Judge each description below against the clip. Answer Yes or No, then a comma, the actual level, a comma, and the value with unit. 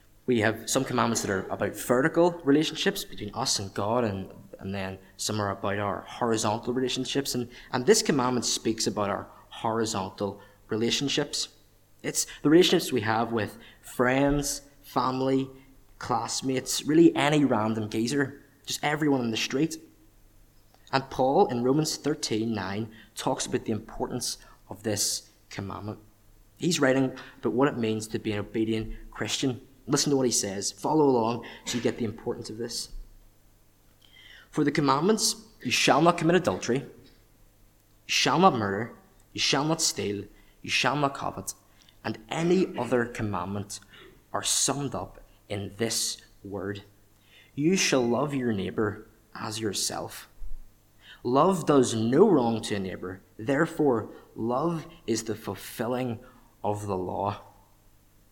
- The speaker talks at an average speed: Yes, average, 145 wpm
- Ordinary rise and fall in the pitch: Yes, average, 4.4 semitones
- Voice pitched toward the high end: No, low, 115 Hz